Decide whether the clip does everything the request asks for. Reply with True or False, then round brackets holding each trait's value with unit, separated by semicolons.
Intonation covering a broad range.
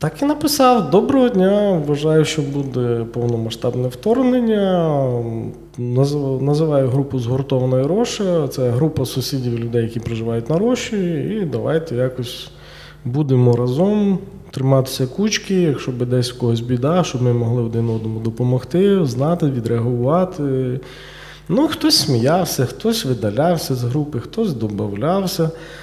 True (6.4 semitones)